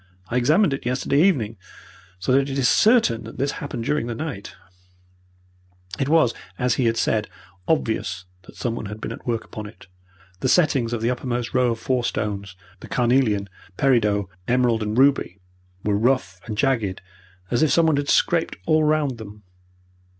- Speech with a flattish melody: No, average, 4.2 semitones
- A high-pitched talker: No, low, 120 Hz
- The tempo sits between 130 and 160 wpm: No, average, 175 wpm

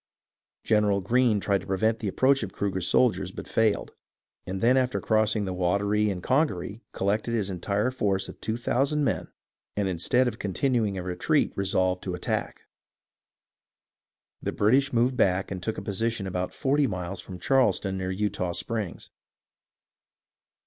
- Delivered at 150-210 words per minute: Yes, average, 155 wpm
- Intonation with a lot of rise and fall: No, average, 3.7 semitones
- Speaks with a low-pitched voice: Yes, low, 100 Hz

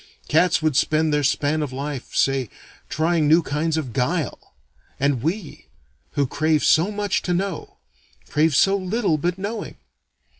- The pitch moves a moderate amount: Yes, average, 3.7 semitones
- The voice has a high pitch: No, medium, 155 Hz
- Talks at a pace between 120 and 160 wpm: Yes, average, 150 wpm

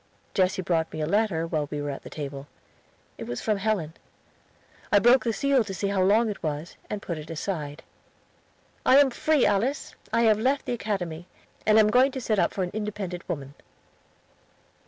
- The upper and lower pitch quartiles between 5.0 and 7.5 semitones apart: Yes, wide, 5.4 semitones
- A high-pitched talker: Yes, high, 195 Hz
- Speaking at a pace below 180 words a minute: No, average, 195 wpm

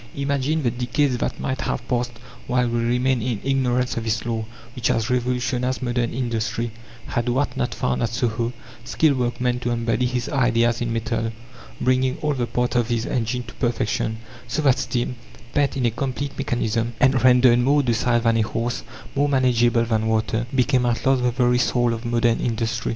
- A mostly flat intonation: Yes, narrow, 1.6 semitones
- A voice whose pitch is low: Yes, low, 120 Hz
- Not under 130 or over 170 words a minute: No, average, 185 wpm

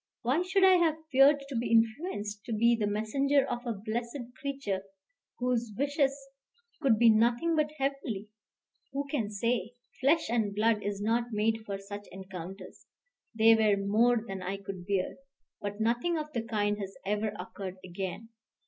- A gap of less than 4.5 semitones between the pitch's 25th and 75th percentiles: No, average, 4.8 semitones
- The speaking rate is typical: Yes, average, 165 wpm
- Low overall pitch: No, high, 225 Hz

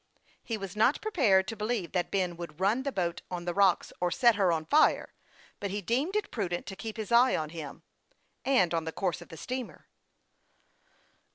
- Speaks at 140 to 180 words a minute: No, average, 200 wpm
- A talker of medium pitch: No, high, 195 Hz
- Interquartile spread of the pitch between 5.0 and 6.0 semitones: Yes, average, 5.3 semitones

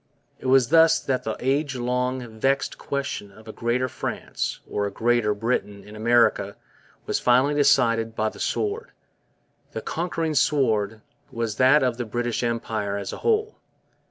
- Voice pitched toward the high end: No, low, 120 Hz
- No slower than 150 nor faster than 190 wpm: Yes, average, 155 wpm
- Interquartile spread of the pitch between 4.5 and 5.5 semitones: No, average, 3.7 semitones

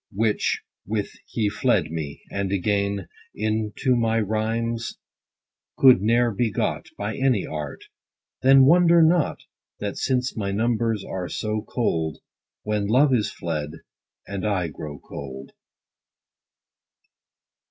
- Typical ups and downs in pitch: Yes, average, 3.5 semitones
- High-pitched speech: No, low, 105 Hz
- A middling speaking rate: No, slow, 120 wpm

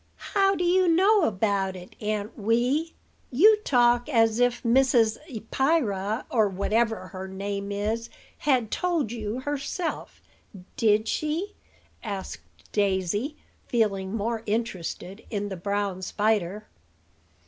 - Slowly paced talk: Yes, slow, 115 wpm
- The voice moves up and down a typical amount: Yes, average, 4.8 semitones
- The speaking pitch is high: Yes, high, 225 Hz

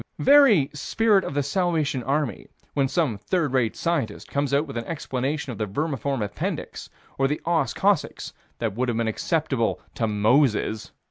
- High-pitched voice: No, medium, 140 Hz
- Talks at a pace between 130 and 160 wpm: No, average, 170 wpm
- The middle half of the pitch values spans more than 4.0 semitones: Yes, average, 5.1 semitones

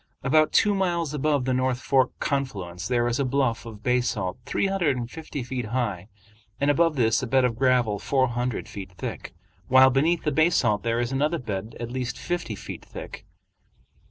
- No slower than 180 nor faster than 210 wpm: Yes, average, 185 wpm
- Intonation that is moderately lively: Yes, average, 3.6 semitones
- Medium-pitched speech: No, low, 130 Hz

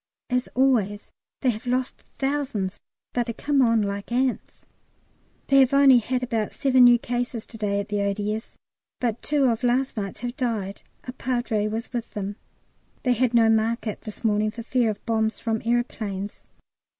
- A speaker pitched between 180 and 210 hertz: No, high, 230 Hz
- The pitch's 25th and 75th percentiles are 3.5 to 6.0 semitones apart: No, average, 2.8 semitones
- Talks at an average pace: Yes, average, 175 wpm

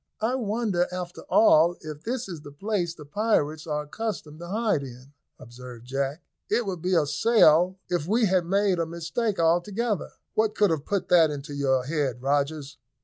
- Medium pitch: Yes, medium, 170 Hz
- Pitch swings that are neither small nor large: No, wide, 5.8 semitones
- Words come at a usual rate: Yes, average, 180 wpm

